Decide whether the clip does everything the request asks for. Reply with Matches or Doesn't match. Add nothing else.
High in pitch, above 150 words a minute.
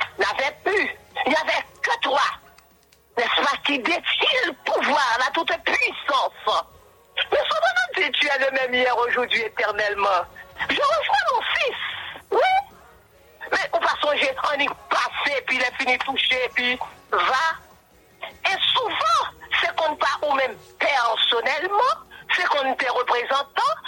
Doesn't match